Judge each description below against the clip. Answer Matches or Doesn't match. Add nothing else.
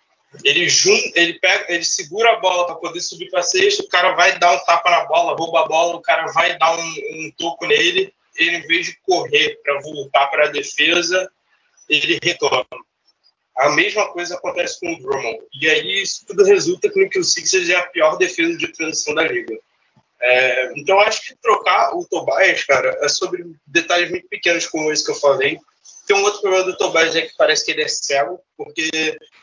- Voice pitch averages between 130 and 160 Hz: Doesn't match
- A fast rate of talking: Matches